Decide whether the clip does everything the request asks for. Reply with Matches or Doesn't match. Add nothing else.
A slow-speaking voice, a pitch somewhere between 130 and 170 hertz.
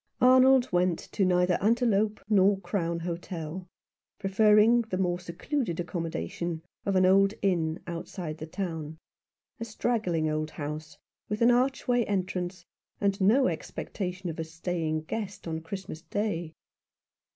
Doesn't match